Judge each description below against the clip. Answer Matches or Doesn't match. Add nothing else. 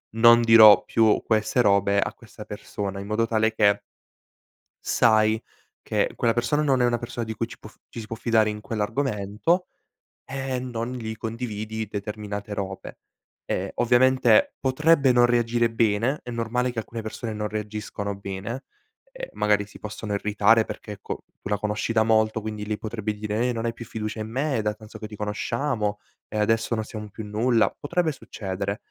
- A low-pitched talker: Matches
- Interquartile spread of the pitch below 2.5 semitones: Matches